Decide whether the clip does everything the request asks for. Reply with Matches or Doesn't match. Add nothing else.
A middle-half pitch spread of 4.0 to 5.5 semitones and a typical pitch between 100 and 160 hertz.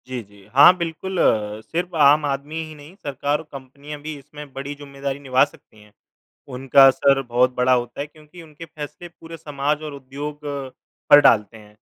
Doesn't match